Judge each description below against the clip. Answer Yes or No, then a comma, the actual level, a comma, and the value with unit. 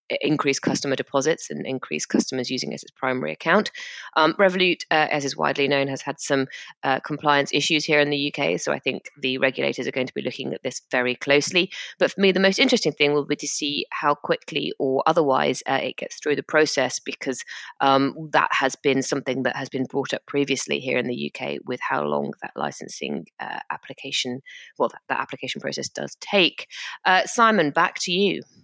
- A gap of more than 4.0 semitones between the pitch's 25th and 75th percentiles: No, average, 3.1 semitones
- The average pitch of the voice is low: No, medium, 145 Hz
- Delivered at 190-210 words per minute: Yes, fast, 205 wpm